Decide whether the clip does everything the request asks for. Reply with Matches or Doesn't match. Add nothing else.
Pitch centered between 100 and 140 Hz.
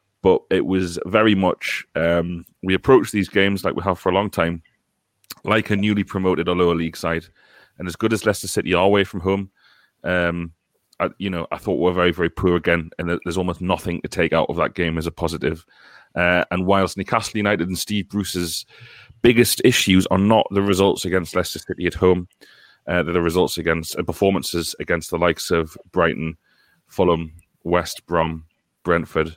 Doesn't match